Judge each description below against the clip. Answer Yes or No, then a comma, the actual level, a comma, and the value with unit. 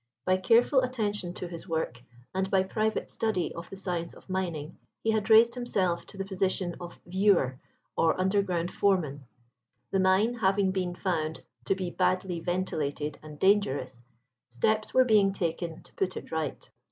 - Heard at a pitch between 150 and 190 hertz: Yes, medium, 185 Hz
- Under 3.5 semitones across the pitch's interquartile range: Yes, average, 3.0 semitones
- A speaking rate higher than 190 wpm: No, average, 165 wpm